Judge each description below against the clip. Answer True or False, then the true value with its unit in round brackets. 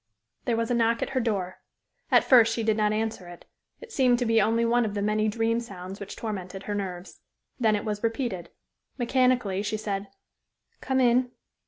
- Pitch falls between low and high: False (220 Hz)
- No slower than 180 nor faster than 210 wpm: True (195 wpm)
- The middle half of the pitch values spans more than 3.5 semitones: False (2.7 semitones)